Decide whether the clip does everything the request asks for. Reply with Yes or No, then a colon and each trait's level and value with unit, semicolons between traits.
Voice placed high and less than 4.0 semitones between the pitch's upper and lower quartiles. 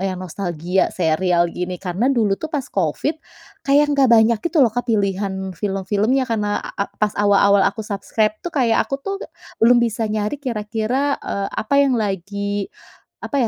Yes: high, 210 Hz; average, 3.5 semitones